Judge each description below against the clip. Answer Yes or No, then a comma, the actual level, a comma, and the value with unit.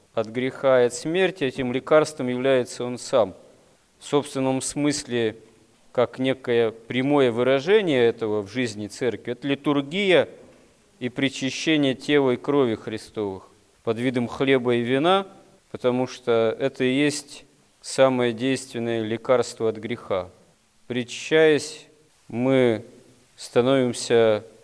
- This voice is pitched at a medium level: No, low, 130 Hz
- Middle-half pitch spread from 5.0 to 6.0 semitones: No, average, 2.9 semitones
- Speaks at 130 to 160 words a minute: No, average, 115 wpm